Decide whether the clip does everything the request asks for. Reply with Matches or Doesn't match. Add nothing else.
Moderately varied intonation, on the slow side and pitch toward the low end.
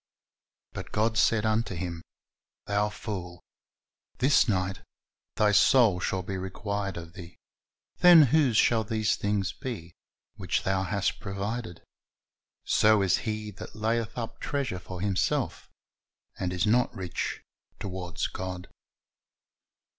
Matches